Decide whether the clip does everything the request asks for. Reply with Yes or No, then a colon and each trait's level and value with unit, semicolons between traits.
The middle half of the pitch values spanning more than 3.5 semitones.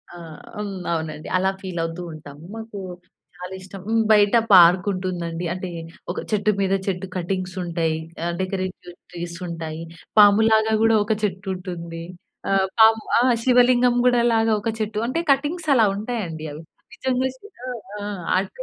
Yes: average, 4.2 semitones